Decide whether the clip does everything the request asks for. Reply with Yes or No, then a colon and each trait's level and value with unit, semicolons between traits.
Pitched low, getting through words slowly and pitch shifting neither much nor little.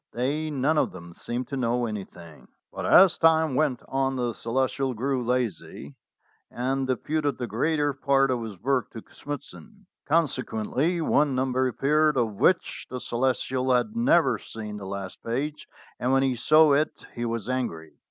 No: low, 130 Hz; average, 165 wpm; average, 3.7 semitones